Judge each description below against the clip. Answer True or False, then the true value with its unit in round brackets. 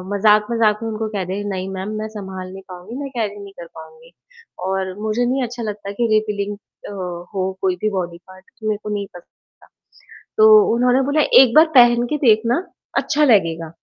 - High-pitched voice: True (210 Hz)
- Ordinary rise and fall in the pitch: True (3.7 semitones)